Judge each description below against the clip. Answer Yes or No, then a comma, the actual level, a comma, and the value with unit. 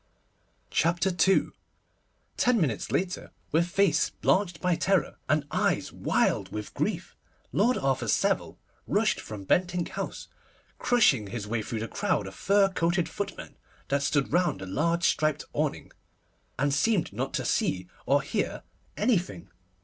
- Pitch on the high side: No, medium, 165 Hz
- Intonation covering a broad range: Yes, wide, 6.7 semitones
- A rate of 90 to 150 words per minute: Yes, average, 140 wpm